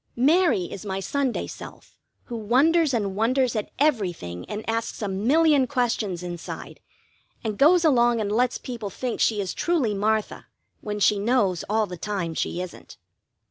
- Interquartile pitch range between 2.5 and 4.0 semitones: No, average, 4.5 semitones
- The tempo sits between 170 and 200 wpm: No, average, 160 wpm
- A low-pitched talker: No, high, 220 Hz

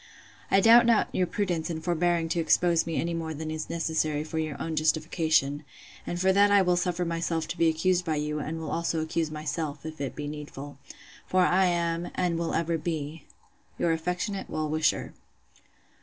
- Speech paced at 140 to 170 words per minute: No, average, 190 wpm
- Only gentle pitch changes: Yes, narrow, 2.0 semitones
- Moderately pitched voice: Yes, medium, 165 Hz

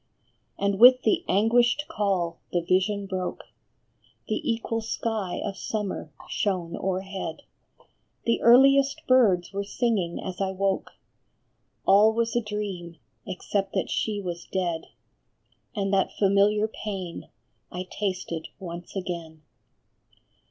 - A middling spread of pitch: Yes, average, 3.2 semitones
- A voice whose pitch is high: Yes, high, 195 Hz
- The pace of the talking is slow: Yes, slow, 120 wpm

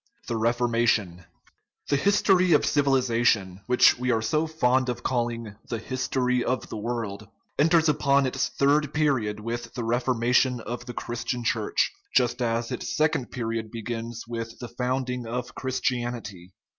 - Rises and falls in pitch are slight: Yes, narrow, 2.1 semitones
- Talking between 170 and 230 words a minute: No, average, 145 wpm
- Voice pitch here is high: No, low, 120 Hz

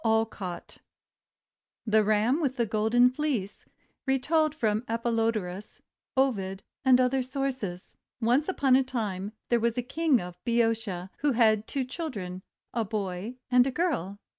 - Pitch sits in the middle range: No, high, 230 Hz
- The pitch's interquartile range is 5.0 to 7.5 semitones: No, average, 4.0 semitones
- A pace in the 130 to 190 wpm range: Yes, average, 140 wpm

